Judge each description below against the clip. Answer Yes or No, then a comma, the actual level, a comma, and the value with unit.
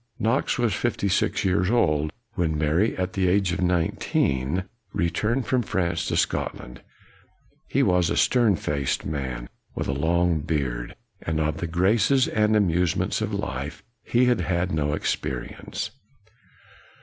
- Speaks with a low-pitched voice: Yes, very low, 90 Hz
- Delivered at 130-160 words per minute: Yes, average, 140 wpm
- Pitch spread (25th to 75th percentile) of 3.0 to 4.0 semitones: No, average, 4.8 semitones